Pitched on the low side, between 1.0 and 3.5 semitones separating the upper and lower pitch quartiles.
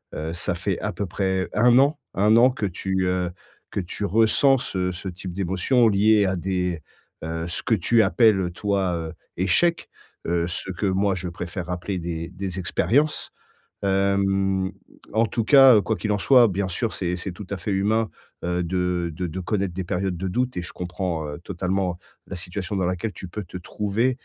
Yes: very low, 95 Hz; average, 2.8 semitones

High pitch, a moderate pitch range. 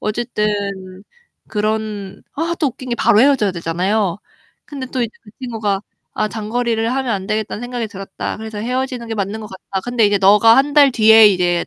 Yes: high, 220 Hz; average, 3.1 semitones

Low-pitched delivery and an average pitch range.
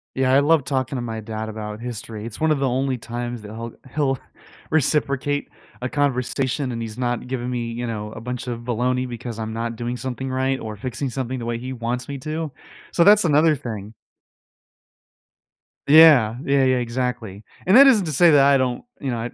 Yes: low, 125 Hz; average, 3.0 semitones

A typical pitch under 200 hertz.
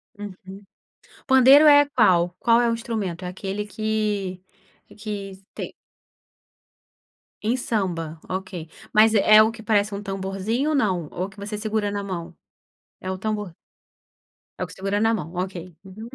No: high, 205 Hz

